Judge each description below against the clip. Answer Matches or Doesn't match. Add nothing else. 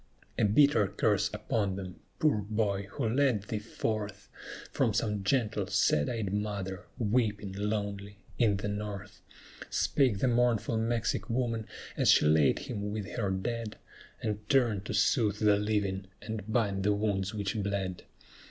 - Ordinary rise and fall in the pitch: Doesn't match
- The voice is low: Matches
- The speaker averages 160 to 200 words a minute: Doesn't match